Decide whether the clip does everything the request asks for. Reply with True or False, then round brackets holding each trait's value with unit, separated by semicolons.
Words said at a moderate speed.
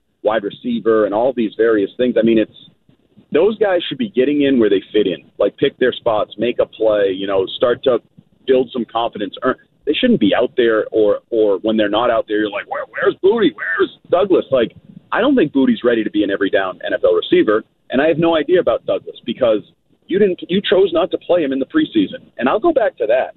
False (235 wpm)